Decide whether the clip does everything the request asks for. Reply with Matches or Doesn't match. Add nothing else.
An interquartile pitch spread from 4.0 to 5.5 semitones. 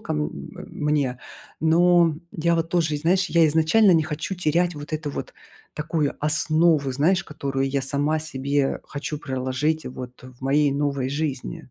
Doesn't match